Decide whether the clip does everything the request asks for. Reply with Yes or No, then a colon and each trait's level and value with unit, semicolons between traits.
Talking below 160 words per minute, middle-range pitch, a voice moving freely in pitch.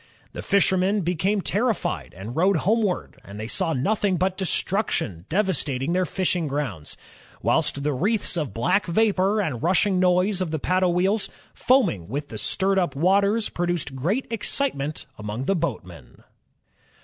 Yes: average, 150 wpm; medium, 180 Hz; wide, 5.9 semitones